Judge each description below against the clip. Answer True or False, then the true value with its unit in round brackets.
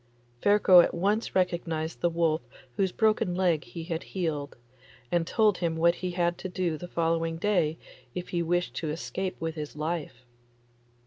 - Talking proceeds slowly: False (170 wpm)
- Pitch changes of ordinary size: False (2.1 semitones)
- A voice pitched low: False (170 Hz)